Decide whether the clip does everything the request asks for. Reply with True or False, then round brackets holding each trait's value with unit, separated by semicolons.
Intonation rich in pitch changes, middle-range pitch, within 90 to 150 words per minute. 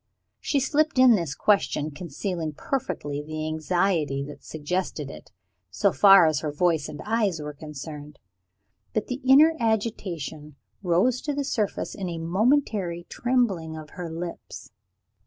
True (6.2 semitones; 175 Hz; 145 wpm)